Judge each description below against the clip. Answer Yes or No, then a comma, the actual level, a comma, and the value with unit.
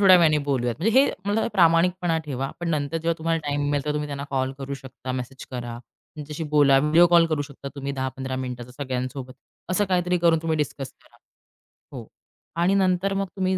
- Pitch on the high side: No, medium, 150 Hz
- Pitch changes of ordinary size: Yes, average, 4.4 semitones